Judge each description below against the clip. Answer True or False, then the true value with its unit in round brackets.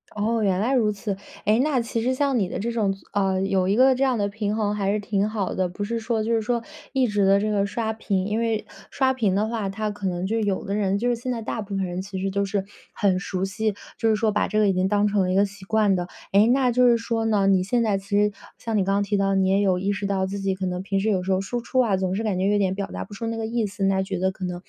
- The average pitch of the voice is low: False (205 Hz)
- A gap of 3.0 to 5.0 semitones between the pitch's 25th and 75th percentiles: False (2.6 semitones)